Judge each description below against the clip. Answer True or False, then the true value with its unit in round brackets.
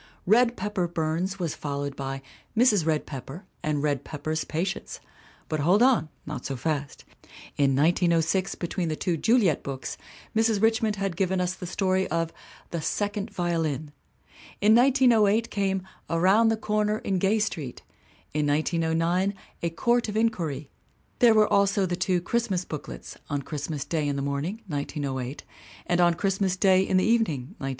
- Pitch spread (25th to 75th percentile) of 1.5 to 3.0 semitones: False (5.1 semitones)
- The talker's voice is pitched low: False (180 Hz)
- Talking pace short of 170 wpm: True (160 wpm)